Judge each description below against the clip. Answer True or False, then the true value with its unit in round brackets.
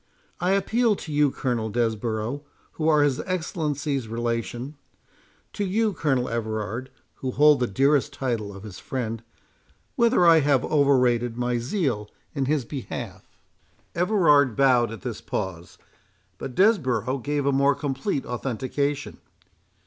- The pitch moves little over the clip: False (4.0 semitones)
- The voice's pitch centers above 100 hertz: True (135 Hz)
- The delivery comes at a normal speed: False (130 wpm)